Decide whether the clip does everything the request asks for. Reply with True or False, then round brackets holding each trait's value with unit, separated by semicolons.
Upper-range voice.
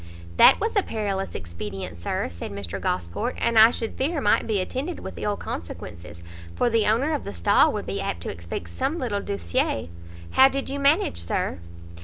True (200 Hz)